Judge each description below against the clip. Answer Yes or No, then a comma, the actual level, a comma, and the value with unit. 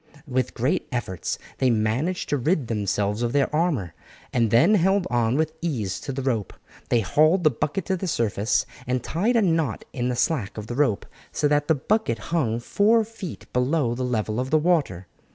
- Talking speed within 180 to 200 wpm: Yes, average, 195 wpm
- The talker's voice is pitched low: Yes, low, 130 Hz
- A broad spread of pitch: Yes, wide, 6.2 semitones